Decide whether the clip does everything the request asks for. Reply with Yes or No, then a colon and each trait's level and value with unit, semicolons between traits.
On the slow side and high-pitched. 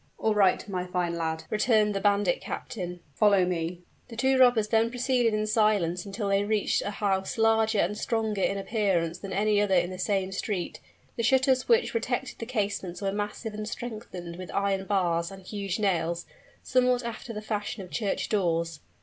No: average, 185 wpm; high, 205 Hz